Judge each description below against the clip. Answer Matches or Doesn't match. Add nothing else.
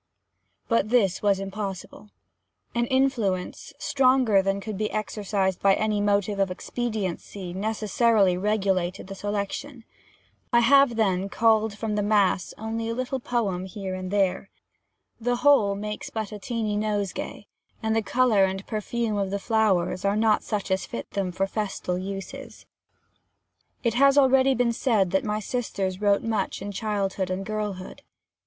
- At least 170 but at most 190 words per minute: Doesn't match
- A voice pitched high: Matches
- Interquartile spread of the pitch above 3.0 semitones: Doesn't match